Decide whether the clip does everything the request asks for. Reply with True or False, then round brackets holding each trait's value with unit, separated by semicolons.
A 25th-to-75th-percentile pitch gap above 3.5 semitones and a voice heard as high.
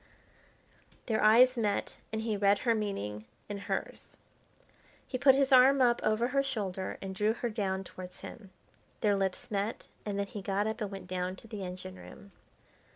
False (3.1 semitones; 205 Hz)